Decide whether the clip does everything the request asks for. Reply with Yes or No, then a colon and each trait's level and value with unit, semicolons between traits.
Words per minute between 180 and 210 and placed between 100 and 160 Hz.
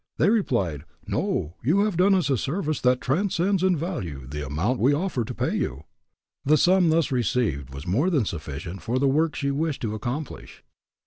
Yes: average, 190 wpm; low, 135 Hz